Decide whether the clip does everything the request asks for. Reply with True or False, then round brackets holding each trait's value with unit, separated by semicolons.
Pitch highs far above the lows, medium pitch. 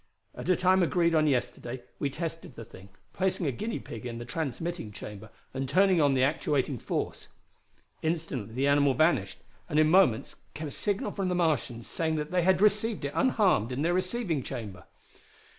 True (5.9 semitones; 155 Hz)